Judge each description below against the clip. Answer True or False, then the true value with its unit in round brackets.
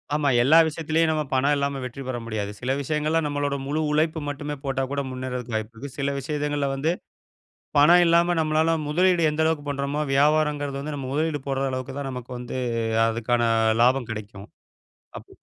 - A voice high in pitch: False (140 Hz)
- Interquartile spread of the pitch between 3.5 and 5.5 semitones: False (3.0 semitones)